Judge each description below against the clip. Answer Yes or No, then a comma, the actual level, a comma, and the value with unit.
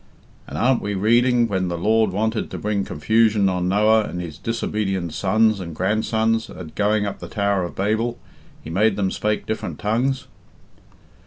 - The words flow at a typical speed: Yes, average, 170 wpm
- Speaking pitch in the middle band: No, low, 105 Hz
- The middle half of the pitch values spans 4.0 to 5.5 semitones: No, average, 2.9 semitones